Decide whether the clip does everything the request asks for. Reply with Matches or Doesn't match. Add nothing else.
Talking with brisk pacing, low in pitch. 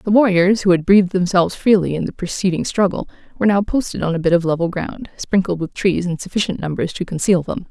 Doesn't match